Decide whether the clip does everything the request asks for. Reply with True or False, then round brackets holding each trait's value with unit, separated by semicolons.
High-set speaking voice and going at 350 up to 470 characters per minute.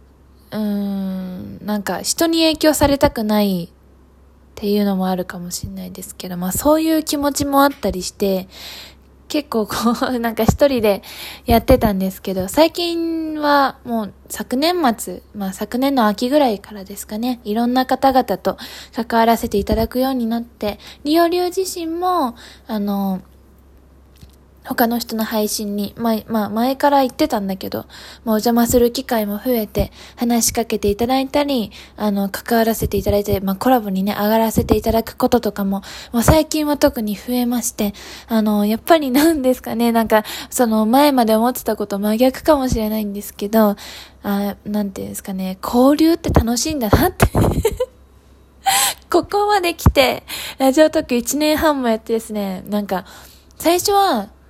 False (225 Hz; 335 characters per minute)